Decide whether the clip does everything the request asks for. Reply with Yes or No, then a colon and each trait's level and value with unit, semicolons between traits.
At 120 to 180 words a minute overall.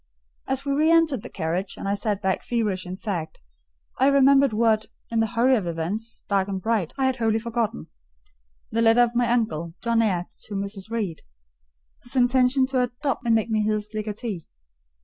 No: average, 190 wpm